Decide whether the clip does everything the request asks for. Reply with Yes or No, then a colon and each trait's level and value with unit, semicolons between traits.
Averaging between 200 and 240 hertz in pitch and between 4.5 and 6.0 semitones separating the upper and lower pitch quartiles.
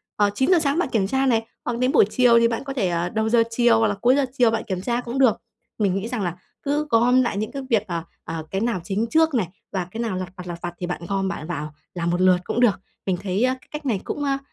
Yes: high, 225 Hz; average, 5.2 semitones